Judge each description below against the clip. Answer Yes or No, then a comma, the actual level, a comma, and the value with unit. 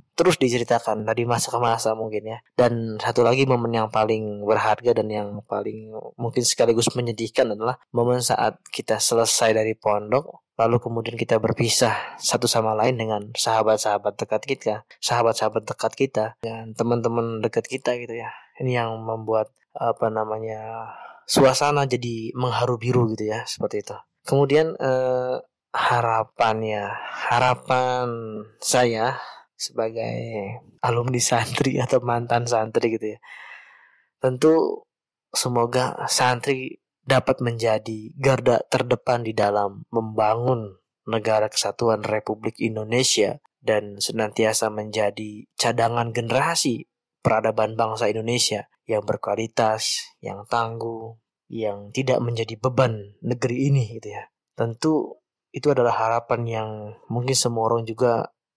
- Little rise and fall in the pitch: Yes, narrow, 2.2 semitones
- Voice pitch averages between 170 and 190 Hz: No, low, 115 Hz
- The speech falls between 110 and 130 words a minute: Yes, average, 120 wpm